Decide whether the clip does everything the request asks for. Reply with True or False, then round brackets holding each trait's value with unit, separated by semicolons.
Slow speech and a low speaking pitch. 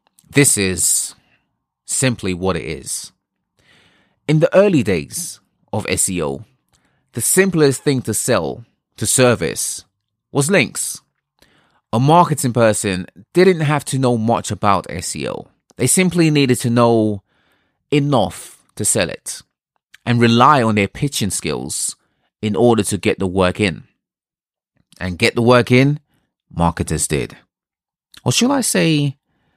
True (130 wpm; 120 Hz)